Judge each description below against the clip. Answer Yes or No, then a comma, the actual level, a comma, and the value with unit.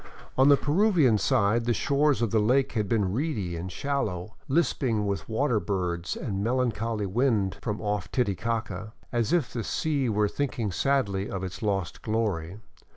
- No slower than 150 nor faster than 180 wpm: Yes, average, 165 wpm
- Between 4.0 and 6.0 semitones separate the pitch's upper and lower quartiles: Yes, average, 4.7 semitones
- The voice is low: Yes, low, 110 Hz